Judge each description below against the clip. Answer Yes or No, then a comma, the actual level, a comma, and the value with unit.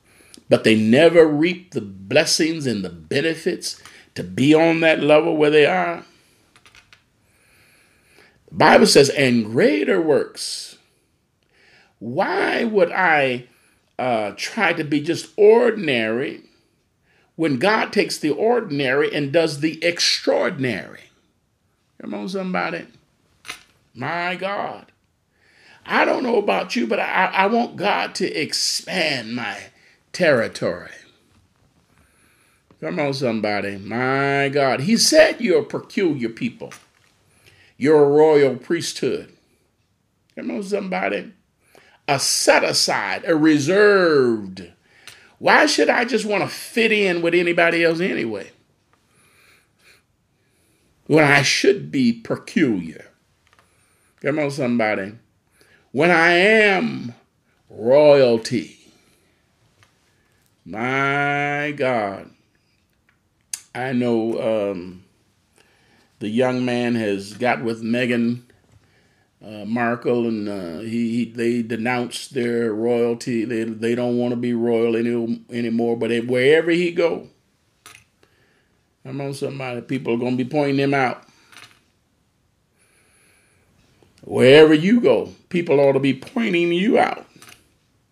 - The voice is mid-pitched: No, low, 130 Hz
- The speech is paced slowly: Yes, slow, 110 wpm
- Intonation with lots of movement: Yes, wide, 6.3 semitones